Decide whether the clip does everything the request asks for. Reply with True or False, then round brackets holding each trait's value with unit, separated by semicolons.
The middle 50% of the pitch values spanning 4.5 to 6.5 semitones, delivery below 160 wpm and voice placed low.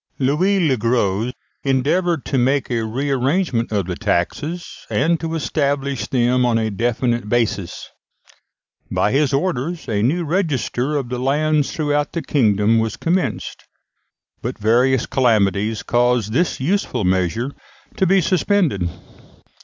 True (5.2 semitones; 135 wpm; 130 Hz)